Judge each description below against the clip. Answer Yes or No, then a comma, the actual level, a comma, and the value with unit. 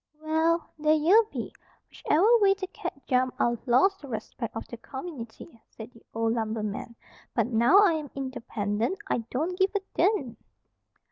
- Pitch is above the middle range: Yes, very high, 265 Hz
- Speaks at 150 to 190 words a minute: Yes, average, 160 wpm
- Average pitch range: No, wide, 6.7 semitones